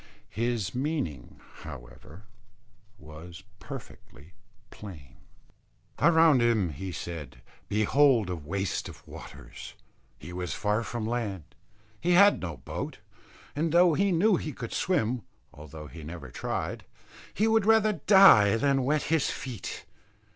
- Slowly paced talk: Yes, slow, 125 wpm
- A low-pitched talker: Yes, low, 110 Hz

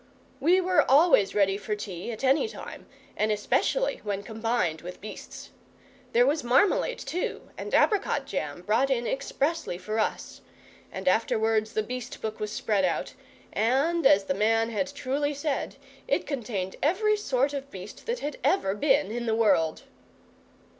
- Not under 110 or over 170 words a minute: Yes, average, 160 wpm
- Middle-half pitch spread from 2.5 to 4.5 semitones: No, wide, 5.6 semitones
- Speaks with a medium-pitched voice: No, high, 230 Hz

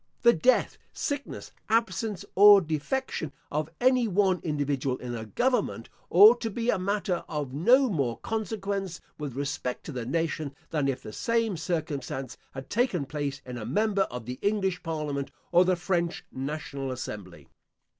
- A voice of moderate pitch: Yes, medium, 165 Hz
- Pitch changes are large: Yes, wide, 7.1 semitones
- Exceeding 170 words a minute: No, average, 155 wpm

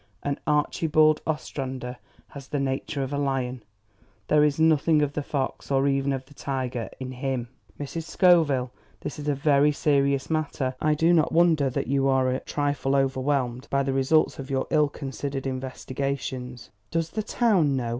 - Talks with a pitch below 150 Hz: Yes, medium, 140 Hz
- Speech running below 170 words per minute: No, average, 175 wpm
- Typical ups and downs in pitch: No, narrow, 2.2 semitones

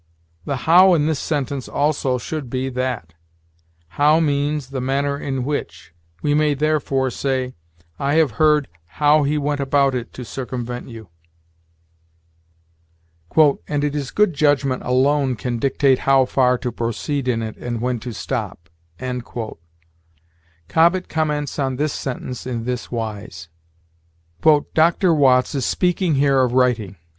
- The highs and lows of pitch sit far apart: No, average, 2.9 semitones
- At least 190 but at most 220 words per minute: No, average, 140 wpm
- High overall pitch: No, low, 135 Hz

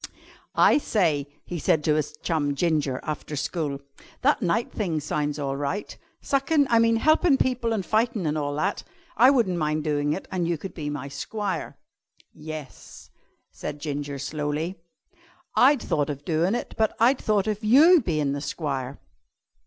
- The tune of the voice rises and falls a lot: Yes, wide, 6.9 semitones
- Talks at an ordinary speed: Yes, average, 165 wpm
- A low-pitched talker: No, medium, 160 Hz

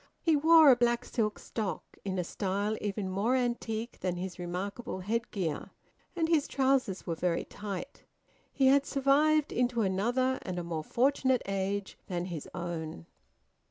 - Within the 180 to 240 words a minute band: No, average, 155 wpm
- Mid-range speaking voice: No, high, 215 Hz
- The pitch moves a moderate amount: No, wide, 5.8 semitones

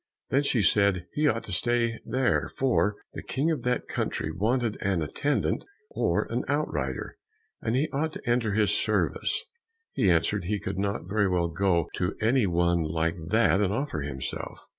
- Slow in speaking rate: No, average, 175 wpm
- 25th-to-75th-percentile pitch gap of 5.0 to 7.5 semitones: Yes, wide, 5.5 semitones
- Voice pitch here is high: No, low, 105 Hz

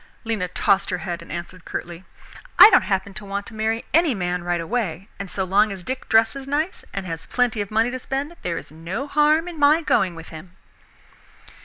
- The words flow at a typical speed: No, fast, 210 wpm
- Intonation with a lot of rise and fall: Yes, wide, 6.3 semitones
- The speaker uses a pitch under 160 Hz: No, high, 200 Hz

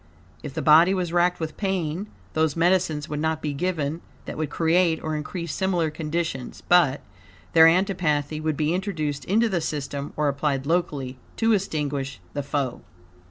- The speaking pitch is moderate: Yes, medium, 160 Hz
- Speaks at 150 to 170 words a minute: Yes, average, 160 wpm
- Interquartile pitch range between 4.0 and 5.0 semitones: No, average, 3.2 semitones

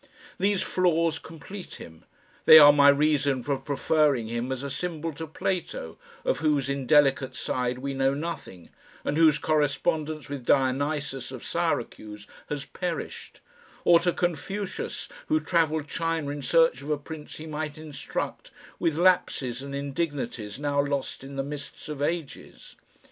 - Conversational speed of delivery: Yes, average, 150 wpm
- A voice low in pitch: No, medium, 145 Hz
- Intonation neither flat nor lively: Yes, average, 3.0 semitones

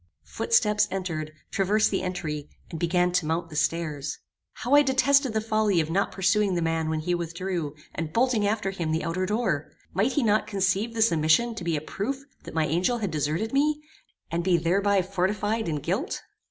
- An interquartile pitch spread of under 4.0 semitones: No, average, 4.7 semitones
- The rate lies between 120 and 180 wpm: No, average, 195 wpm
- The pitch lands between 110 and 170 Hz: No, medium, 185 Hz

